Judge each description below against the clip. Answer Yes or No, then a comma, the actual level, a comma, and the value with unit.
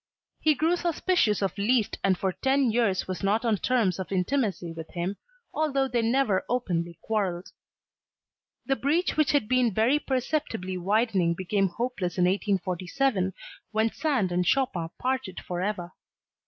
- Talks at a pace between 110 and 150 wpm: Yes, average, 145 wpm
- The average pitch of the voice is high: Yes, high, 210 Hz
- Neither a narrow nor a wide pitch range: No, wide, 6.1 semitones